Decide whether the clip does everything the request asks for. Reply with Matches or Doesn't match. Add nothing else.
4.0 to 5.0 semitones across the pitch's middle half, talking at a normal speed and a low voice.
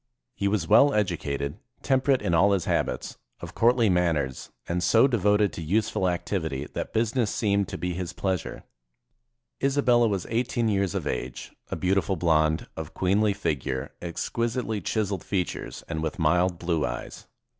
Matches